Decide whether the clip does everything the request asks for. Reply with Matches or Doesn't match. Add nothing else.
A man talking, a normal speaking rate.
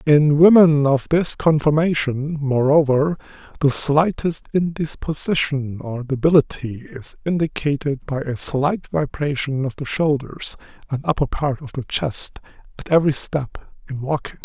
Doesn't match